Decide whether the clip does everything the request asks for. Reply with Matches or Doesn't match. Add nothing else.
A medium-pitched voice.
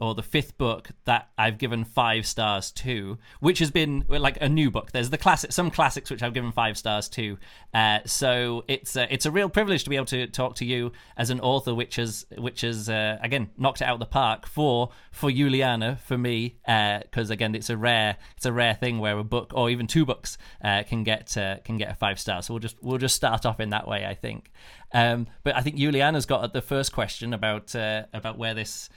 Doesn't match